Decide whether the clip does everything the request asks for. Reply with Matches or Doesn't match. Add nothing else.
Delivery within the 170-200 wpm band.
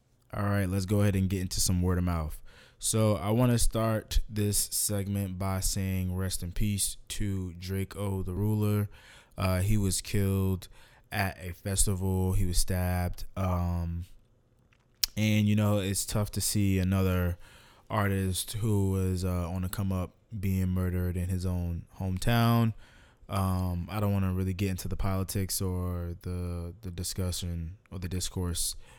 Doesn't match